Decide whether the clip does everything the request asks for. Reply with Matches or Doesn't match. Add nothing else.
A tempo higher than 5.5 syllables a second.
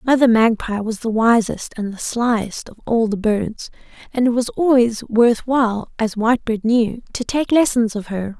Doesn't match